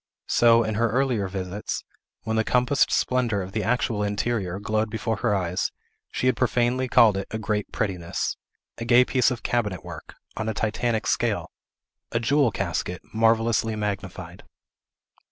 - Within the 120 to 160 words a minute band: Yes, average, 155 wpm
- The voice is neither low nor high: No, low, 110 Hz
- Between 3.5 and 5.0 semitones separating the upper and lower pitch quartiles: No, average, 3.0 semitones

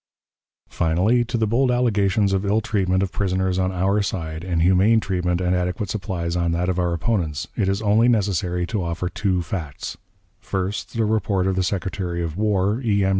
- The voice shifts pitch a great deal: No, average, 2.8 semitones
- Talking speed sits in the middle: Yes, average, 190 wpm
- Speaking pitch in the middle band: No, very low, 95 Hz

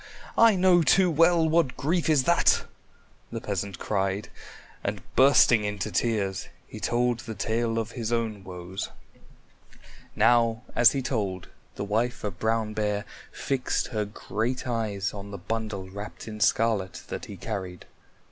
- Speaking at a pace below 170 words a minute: Yes, average, 145 wpm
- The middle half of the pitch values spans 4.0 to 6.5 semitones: No, average, 3.5 semitones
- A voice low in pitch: Yes, low, 110 Hz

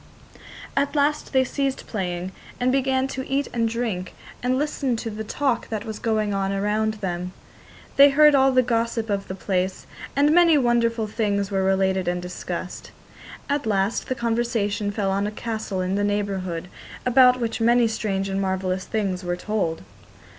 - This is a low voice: No, high, 220 Hz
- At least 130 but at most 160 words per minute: No, average, 170 wpm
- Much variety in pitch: No, average, 4.5 semitones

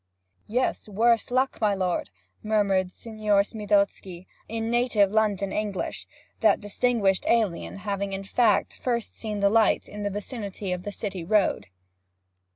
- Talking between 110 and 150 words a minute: Yes, average, 140 wpm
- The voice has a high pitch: Yes, high, 205 Hz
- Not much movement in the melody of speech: Yes, narrow, 2.3 semitones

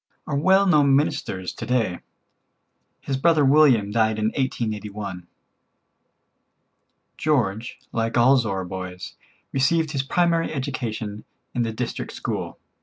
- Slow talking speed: Yes, slow, 115 wpm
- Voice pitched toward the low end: Yes, low, 120 Hz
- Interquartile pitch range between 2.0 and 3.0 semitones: No, average, 5.1 semitones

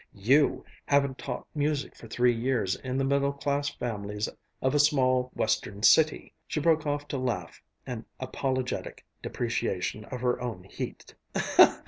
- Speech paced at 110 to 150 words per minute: Yes, average, 145 wpm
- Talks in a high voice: No, low, 130 Hz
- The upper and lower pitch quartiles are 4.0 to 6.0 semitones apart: No, average, 3.2 semitones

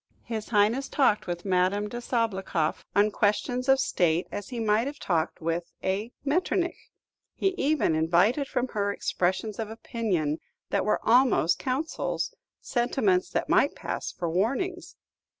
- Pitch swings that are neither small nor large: No, wide, 5.9 semitones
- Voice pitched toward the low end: No, high, 215 Hz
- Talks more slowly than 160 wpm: Yes, average, 145 wpm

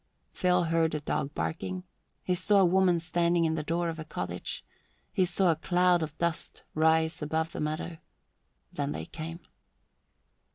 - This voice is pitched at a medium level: Yes, medium, 165 Hz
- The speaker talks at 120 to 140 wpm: No, average, 165 wpm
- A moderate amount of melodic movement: No, narrow, 1.9 semitones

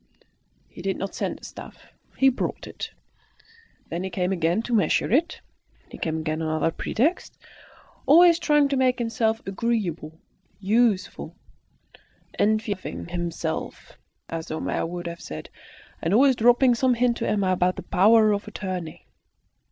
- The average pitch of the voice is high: Yes, high, 205 Hz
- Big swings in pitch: Yes, wide, 5.8 semitones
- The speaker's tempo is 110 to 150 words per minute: Yes, average, 145 wpm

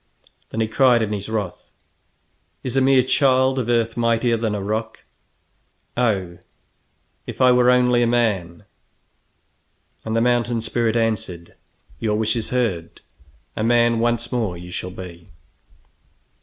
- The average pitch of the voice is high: No, low, 115 Hz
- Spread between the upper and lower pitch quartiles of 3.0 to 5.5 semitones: No, narrow, 2.4 semitones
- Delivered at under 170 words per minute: Yes, average, 140 wpm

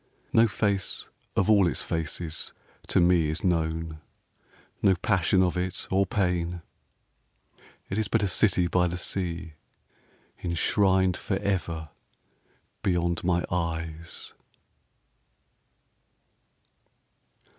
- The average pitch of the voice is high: No, very low, 90 Hz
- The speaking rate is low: Yes, slow, 100 wpm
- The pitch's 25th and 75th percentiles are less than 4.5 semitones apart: Yes, narrow, 2.4 semitones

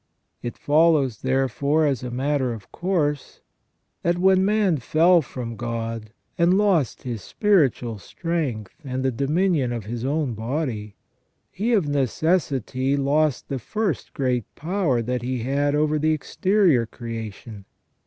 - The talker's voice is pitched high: No, medium, 140 Hz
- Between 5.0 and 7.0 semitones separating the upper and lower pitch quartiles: Yes, average, 5.3 semitones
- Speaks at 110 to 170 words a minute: Yes, slow, 135 wpm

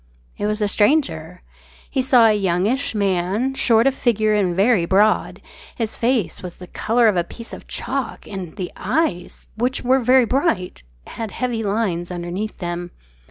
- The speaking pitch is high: Yes, high, 215 Hz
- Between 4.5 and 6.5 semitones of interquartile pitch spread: Yes, average, 5.2 semitones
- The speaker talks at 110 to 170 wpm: Yes, average, 165 wpm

